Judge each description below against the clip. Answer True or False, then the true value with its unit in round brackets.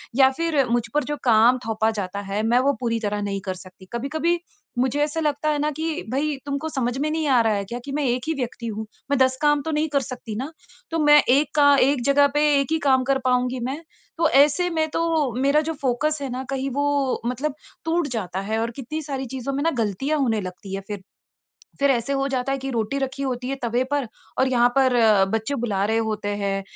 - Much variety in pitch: False (3.8 semitones)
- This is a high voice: True (265 Hz)